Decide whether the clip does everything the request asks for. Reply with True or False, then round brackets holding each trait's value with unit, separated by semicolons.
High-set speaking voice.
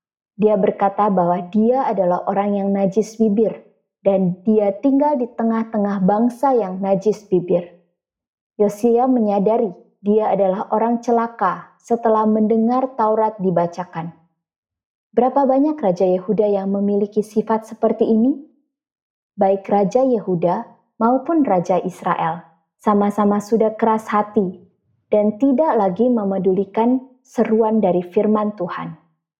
True (210 Hz)